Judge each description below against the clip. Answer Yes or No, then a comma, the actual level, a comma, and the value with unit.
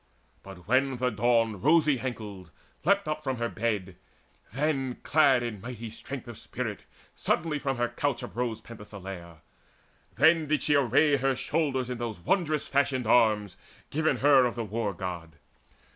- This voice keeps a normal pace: Yes, average, 160 wpm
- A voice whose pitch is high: No, low, 125 Hz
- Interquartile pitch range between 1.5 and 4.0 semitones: No, average, 4.7 semitones